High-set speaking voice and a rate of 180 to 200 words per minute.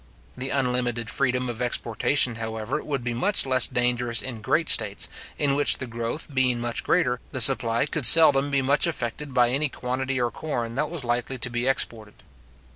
No: low, 125 Hz; average, 185 wpm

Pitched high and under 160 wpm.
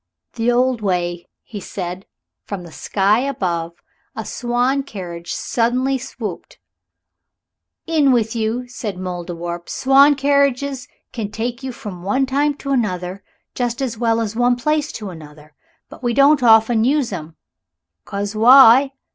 Yes: high, 230 Hz; average, 145 wpm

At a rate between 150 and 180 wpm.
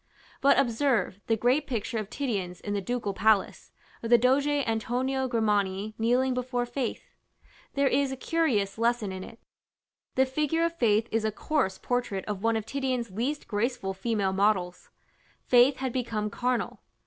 Yes: average, 160 wpm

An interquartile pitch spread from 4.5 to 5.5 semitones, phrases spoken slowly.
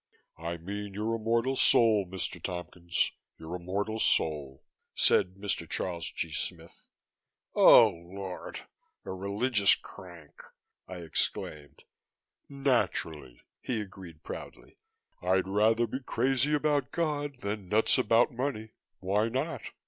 Yes: average, 4.9 semitones; slow, 115 wpm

